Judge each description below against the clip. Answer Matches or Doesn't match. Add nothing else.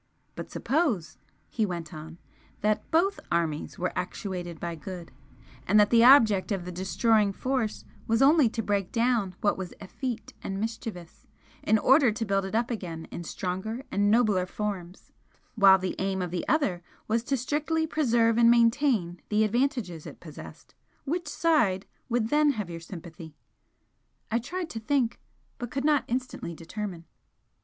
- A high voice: Matches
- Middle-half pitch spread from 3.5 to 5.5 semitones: Matches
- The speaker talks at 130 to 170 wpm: Matches